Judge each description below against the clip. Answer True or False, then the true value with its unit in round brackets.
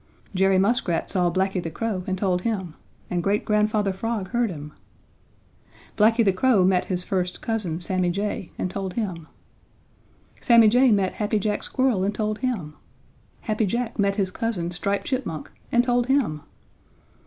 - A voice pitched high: True (200 Hz)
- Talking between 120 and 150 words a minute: False (160 wpm)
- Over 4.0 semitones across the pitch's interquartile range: False (3.7 semitones)